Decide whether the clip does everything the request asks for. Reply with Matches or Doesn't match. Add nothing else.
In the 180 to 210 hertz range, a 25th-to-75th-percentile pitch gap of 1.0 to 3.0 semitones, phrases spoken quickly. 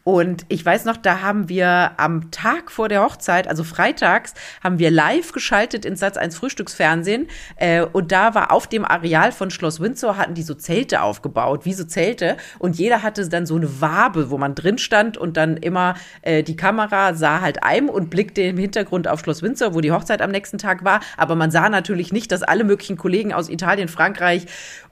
Doesn't match